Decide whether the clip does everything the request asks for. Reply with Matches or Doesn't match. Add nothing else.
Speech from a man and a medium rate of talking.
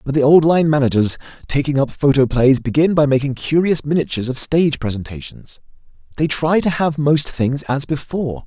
Matches